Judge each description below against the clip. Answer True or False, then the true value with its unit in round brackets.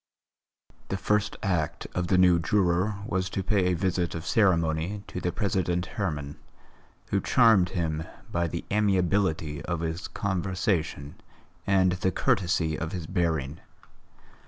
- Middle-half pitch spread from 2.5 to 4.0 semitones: True (2.8 semitones)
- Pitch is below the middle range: True (90 Hz)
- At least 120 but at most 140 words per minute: True (135 wpm)